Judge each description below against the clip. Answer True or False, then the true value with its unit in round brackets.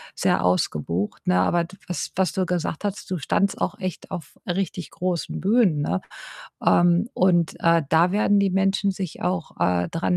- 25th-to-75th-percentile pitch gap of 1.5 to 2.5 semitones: False (2.9 semitones)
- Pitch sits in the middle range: True (180 Hz)